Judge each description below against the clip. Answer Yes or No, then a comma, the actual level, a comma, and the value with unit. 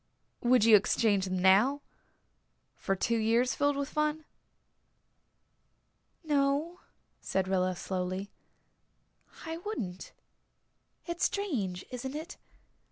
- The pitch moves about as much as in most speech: No, wide, 7.7 semitones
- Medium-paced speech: No, slow, 100 wpm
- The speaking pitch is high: Yes, high, 240 Hz